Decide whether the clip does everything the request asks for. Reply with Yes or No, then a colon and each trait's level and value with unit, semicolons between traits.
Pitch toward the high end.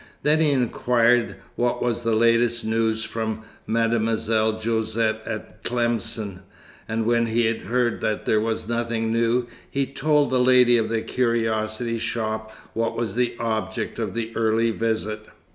No: low, 115 Hz